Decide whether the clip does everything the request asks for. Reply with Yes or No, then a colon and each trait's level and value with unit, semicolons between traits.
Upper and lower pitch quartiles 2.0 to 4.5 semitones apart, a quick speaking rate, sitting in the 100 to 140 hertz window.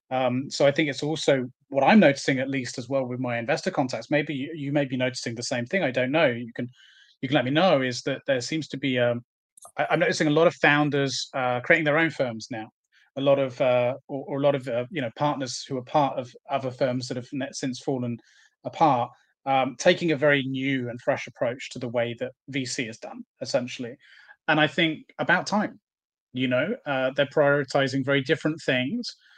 Yes: average, 2.9 semitones; fast, 225 wpm; low, 135 Hz